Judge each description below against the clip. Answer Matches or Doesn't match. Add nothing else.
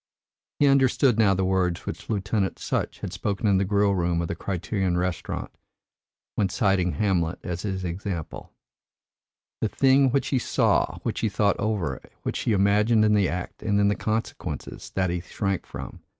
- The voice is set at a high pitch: Doesn't match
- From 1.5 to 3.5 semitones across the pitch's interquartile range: Matches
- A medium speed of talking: Matches